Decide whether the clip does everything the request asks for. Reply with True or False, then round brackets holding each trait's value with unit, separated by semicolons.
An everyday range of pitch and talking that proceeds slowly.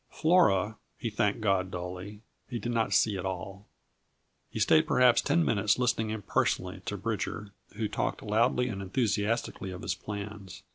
False (3.0 semitones; 155 wpm)